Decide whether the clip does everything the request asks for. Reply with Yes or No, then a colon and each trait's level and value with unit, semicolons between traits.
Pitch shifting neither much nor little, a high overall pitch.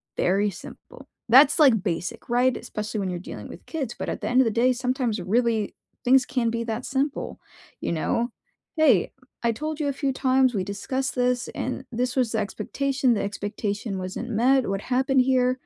Yes: average, 3.8 semitones; high, 245 Hz